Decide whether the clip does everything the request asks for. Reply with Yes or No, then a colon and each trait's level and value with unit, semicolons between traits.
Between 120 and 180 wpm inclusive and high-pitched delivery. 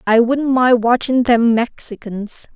Yes: average, 140 wpm; high, 240 Hz